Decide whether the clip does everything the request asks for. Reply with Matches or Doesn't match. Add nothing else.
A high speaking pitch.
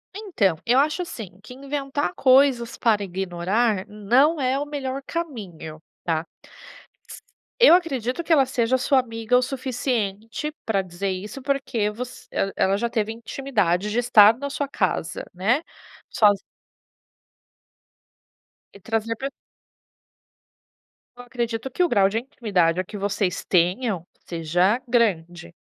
Matches